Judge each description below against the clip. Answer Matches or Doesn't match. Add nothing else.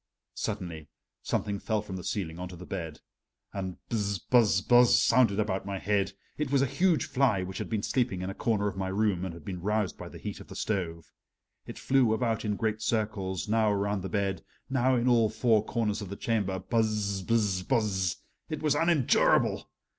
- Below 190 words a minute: Doesn't match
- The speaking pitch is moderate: Doesn't match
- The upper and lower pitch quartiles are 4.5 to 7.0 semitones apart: Doesn't match